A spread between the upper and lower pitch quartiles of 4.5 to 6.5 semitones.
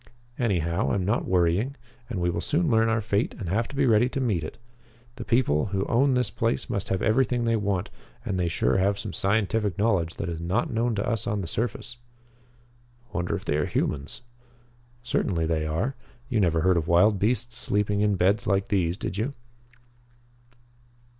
Yes: average, 4.8 semitones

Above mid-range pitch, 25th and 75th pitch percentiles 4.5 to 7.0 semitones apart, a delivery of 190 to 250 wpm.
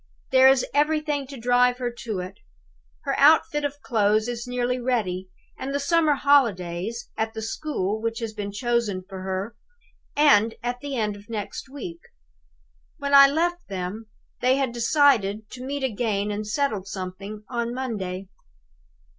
No: high, 235 Hz; average, 5.0 semitones; average, 155 wpm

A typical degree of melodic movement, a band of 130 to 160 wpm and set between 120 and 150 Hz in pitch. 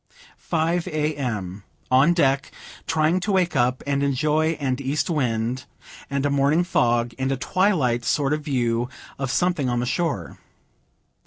Yes: average, 4.1 semitones; average, 155 wpm; medium, 140 Hz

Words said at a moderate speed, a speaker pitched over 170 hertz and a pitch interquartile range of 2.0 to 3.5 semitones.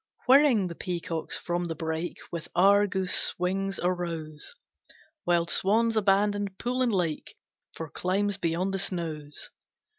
No: slow, 125 wpm; medium, 185 Hz; average, 3.1 semitones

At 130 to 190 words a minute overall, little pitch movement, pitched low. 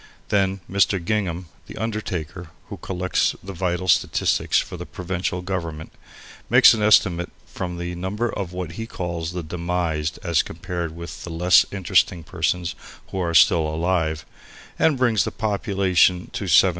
Yes: average, 155 wpm; narrow, 2.2 semitones; very low, 90 Hz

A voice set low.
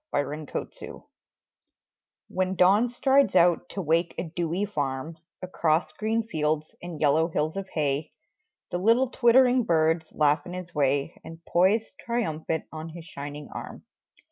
No: medium, 170 Hz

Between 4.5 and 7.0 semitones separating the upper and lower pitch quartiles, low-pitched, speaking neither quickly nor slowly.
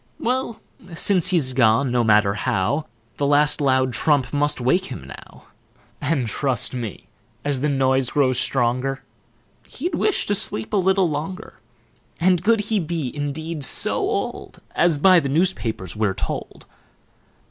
No: wide, 5.6 semitones; medium, 145 Hz; average, 150 wpm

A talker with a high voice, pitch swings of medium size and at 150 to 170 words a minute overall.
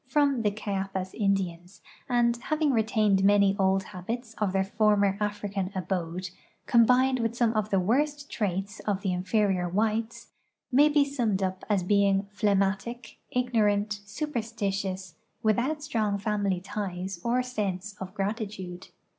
No: high, 205 Hz; average, 3.3 semitones; average, 140 wpm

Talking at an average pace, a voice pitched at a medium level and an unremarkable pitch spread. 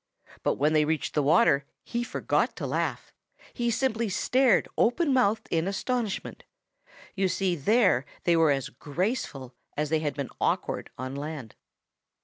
No: average, 150 wpm; medium, 175 Hz; wide, 7.6 semitones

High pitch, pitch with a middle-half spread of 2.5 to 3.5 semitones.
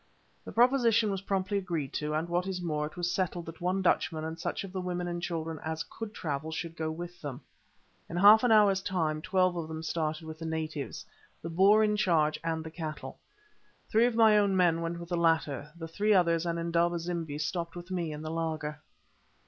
No: medium, 170 Hz; average, 2.8 semitones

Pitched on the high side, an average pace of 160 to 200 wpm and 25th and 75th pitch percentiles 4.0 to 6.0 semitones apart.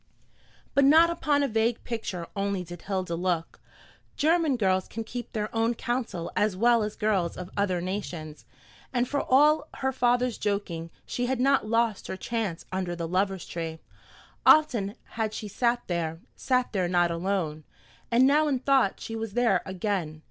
Yes: high, 210 Hz; average, 170 wpm; average, 5.2 semitones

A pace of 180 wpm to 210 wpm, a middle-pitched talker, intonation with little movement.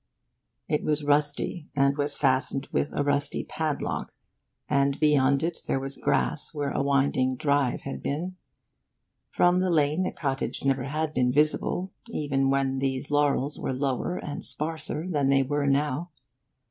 No: average, 155 wpm; medium, 145 Hz; narrow, 1.8 semitones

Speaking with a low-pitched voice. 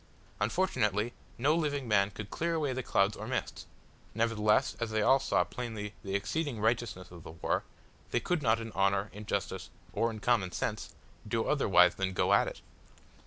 Yes: low, 110 Hz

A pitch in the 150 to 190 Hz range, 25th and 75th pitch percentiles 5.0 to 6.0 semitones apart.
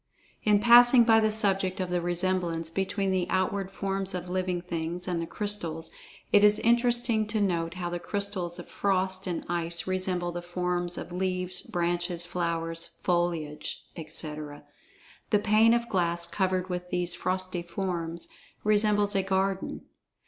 No: medium, 185 Hz; narrow, 2.4 semitones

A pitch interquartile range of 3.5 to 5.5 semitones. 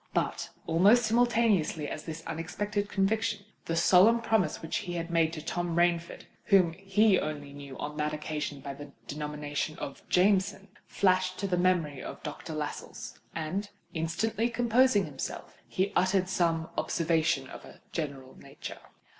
Yes: average, 4.6 semitones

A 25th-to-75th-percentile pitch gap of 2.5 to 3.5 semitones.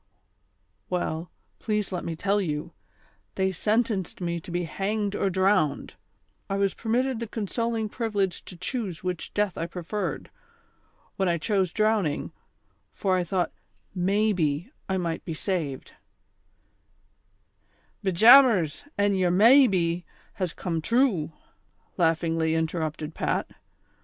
No: average, 3.9 semitones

